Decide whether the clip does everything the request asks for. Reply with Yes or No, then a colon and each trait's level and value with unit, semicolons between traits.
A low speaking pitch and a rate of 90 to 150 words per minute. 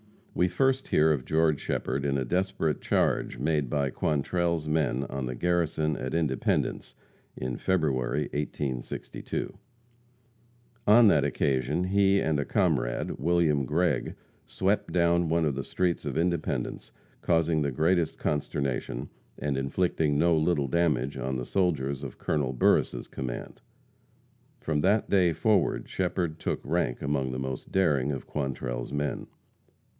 Yes: very low, 75 Hz; average, 140 wpm